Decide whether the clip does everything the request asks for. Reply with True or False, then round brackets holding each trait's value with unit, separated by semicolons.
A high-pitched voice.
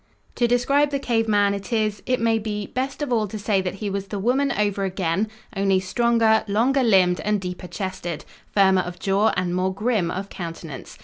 True (205 Hz)